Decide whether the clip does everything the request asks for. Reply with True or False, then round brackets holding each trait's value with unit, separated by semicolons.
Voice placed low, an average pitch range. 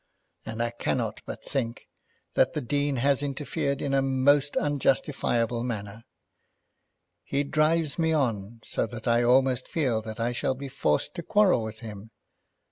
True (130 Hz; 3.7 semitones)